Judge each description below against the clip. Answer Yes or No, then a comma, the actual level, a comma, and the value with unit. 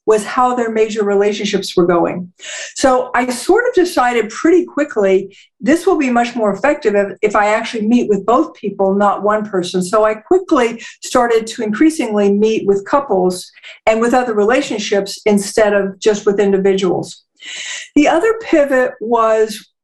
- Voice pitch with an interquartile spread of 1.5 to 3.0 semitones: No, average, 4.2 semitones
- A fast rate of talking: No, average, 160 wpm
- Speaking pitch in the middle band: No, high, 220 Hz